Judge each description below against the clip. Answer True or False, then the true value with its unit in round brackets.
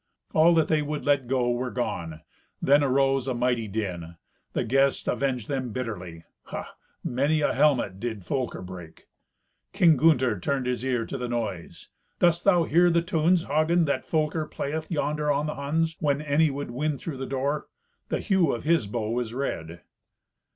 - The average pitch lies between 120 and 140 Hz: True (135 Hz)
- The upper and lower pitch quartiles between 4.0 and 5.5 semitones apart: True (4.3 semitones)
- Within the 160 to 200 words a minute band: True (175 wpm)